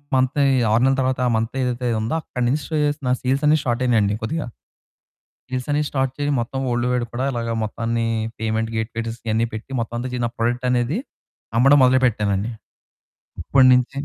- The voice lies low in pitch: Yes, low, 125 Hz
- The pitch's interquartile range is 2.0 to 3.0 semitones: Yes, narrow, 2.4 semitones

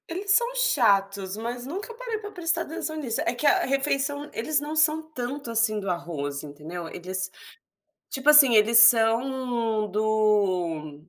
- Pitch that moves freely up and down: Yes, wide, 7.2 semitones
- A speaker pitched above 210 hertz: Yes, high, 235 Hz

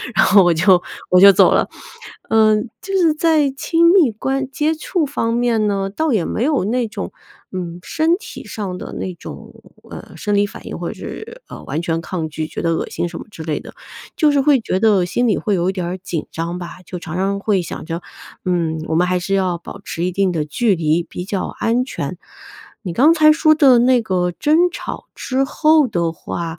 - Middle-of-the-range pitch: No, high, 200 Hz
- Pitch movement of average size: No, wide, 7.4 semitones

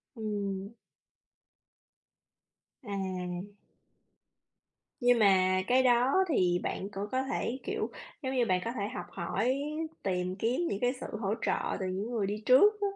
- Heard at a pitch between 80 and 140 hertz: No, high, 210 Hz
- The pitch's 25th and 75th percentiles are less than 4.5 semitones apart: No, average, 4.8 semitones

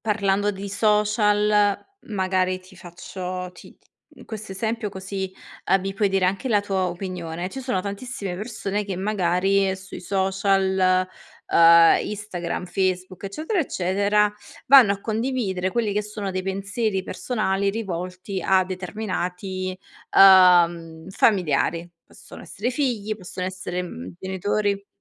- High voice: Yes, high, 195 Hz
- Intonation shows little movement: Yes, narrow, 2.1 semitones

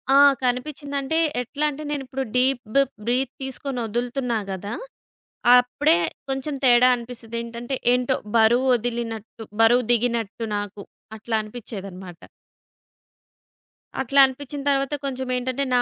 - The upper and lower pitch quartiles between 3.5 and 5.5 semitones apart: No, average, 2.7 semitones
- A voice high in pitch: Yes, high, 245 Hz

